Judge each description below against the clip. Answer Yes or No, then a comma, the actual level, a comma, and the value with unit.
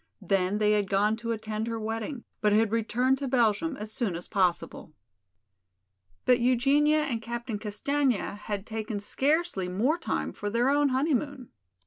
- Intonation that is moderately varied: Yes, average, 4.0 semitones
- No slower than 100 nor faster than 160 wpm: Yes, average, 155 wpm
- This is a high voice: Yes, high, 225 Hz